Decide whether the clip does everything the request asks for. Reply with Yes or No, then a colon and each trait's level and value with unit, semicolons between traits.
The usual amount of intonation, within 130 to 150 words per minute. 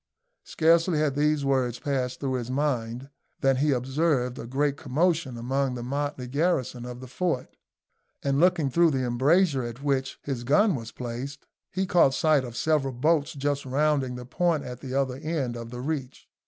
No: average, 3.3 semitones; average, 180 wpm